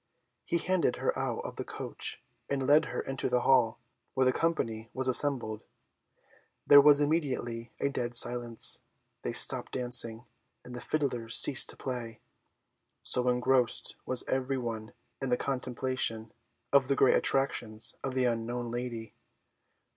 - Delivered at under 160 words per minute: Yes, average, 145 wpm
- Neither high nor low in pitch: No, low, 125 Hz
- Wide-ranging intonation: No, narrow, 2.4 semitones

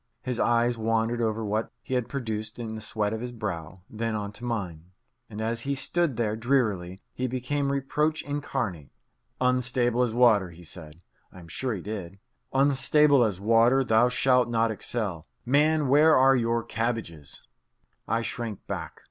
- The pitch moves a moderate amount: Yes, average, 3.2 semitones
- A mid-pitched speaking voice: No, low, 115 Hz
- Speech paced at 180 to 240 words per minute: No, average, 165 wpm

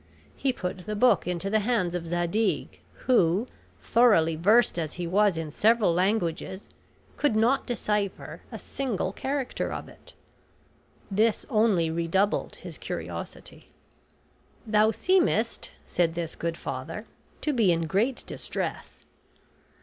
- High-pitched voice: Yes, high, 200 Hz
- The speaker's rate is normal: No, slow, 125 wpm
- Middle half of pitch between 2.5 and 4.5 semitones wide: No, average, 5.0 semitones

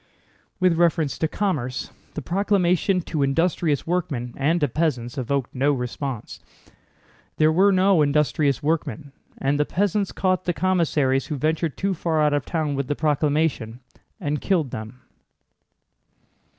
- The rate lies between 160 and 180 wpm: No, average, 140 wpm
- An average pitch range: Yes, average, 4.0 semitones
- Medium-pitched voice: Yes, medium, 150 Hz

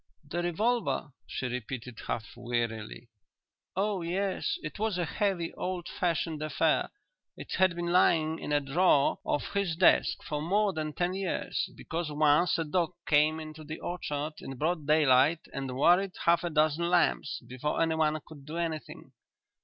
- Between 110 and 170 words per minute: Yes, average, 160 wpm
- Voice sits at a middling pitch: Yes, medium, 160 Hz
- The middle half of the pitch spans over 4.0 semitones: No, average, 3.2 semitones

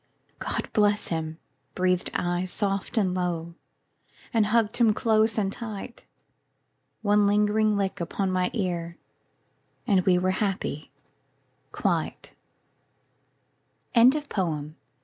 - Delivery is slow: Yes, slow, 105 wpm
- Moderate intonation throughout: Yes, average, 3.2 semitones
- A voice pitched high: Yes, high, 195 Hz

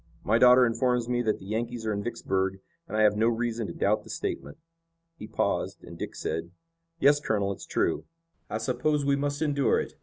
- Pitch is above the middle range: No, low, 115 Hz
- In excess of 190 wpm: Yes, fast, 205 wpm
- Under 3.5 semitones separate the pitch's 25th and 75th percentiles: Yes, average, 3.0 semitones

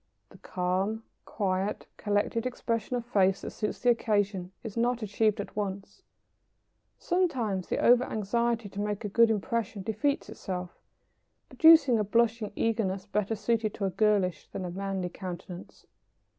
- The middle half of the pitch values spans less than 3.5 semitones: Yes, average, 3.1 semitones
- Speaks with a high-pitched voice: Yes, high, 210 Hz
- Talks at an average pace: Yes, average, 145 wpm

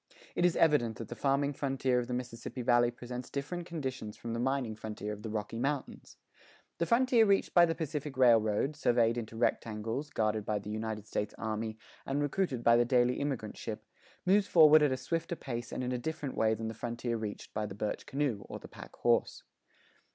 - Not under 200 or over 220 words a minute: Yes, fast, 205 wpm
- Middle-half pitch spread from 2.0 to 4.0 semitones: No, average, 4.5 semitones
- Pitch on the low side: Yes, low, 125 Hz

